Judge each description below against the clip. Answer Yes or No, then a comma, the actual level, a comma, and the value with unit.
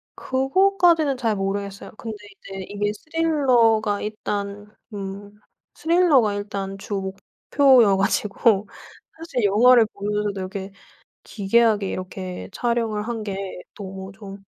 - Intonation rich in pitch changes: No, average, 3.4 semitones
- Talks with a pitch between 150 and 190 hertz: No, high, 210 Hz